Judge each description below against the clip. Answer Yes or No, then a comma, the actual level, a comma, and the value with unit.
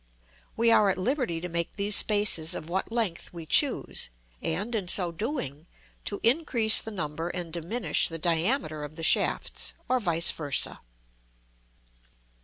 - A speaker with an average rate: Yes, average, 150 wpm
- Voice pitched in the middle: Yes, medium, 180 Hz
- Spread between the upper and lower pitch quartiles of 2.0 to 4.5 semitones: No, average, 5.2 semitones